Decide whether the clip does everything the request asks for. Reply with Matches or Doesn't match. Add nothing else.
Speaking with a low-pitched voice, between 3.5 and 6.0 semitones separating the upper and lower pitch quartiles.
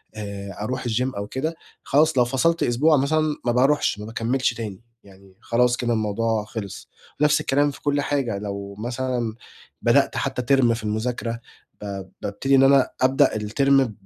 Matches